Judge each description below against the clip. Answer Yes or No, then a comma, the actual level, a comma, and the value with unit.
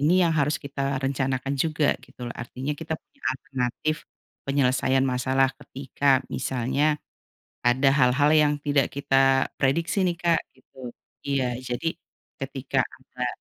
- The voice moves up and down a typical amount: No, narrow, 2.1 semitones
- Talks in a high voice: No, low, 135 Hz